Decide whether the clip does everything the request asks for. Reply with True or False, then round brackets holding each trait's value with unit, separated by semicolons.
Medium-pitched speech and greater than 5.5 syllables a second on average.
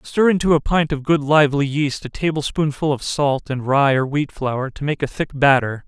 False (145 Hz; 5.0 syllables/s)